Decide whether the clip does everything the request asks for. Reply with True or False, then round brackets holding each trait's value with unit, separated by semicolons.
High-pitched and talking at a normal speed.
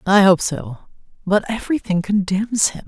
True (195 Hz; 145 wpm)